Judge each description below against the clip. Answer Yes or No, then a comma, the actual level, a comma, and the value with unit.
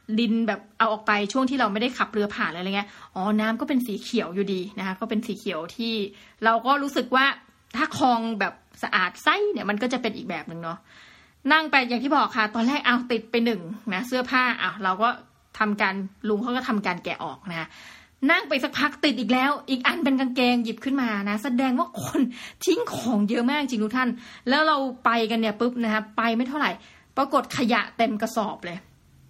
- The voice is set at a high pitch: Yes, high, 230 Hz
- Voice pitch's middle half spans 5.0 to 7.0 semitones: No, average, 3.8 semitones